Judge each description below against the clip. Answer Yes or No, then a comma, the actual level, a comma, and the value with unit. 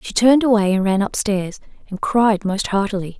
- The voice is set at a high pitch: Yes, high, 205 Hz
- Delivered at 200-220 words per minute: Yes, fast, 205 wpm